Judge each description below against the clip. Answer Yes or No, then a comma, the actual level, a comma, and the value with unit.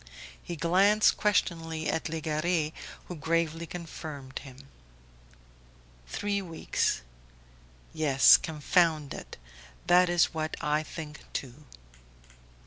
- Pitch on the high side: No, medium, 160 Hz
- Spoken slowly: Yes, slow, 95 wpm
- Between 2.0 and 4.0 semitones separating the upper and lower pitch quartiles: Yes, narrow, 2.5 semitones